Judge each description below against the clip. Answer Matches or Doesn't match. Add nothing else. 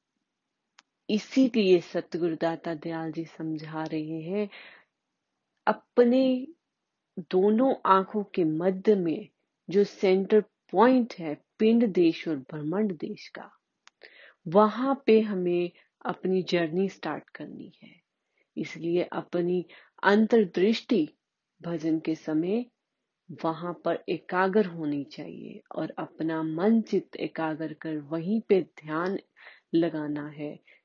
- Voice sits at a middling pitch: Matches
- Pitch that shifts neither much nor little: Matches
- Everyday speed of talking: Doesn't match